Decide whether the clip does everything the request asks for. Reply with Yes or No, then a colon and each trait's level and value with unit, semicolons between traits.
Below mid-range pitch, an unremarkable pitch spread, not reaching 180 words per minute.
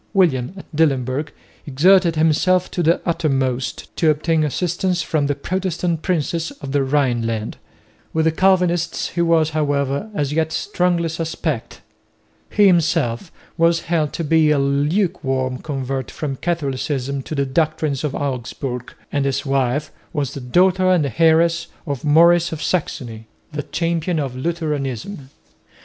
No: medium, 155 Hz; average, 3.8 semitones; average, 140 wpm